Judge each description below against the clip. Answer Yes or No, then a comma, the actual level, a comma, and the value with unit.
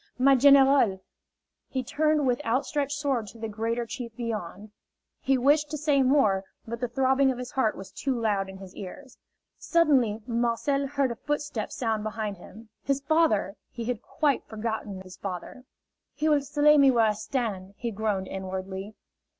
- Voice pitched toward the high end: Yes, high, 235 Hz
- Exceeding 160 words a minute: Yes, average, 170 wpm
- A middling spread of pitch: Yes, average, 4.7 semitones